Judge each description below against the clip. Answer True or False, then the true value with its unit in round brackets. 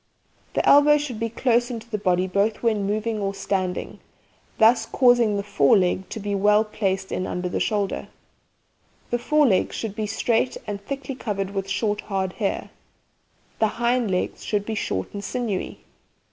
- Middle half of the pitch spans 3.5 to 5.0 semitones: False (3.0 semitones)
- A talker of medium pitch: False (210 Hz)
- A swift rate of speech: False (175 wpm)